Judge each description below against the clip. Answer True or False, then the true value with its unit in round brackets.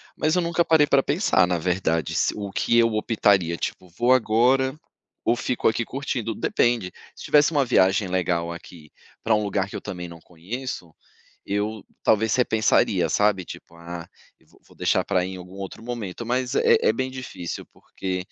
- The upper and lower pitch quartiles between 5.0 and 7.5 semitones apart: True (5.3 semitones)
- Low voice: True (105 Hz)